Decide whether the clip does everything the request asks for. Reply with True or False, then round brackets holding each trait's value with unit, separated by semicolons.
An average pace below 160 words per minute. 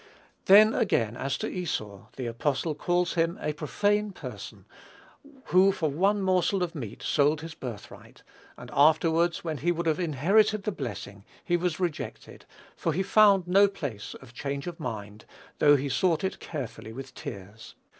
False (165 wpm)